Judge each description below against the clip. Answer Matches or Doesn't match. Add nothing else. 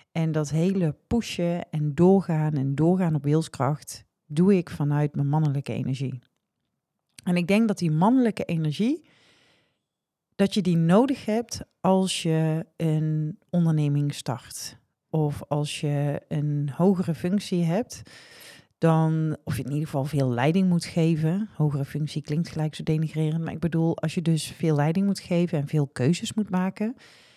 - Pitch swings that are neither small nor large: Matches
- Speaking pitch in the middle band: Matches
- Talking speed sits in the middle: Matches